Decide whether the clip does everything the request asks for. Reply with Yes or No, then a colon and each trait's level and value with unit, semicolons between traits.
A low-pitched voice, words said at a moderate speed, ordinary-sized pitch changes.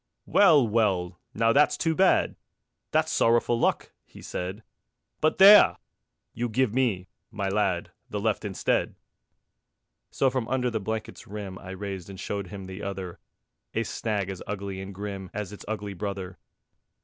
Yes: low, 105 Hz; average, 155 wpm; average, 3.2 semitones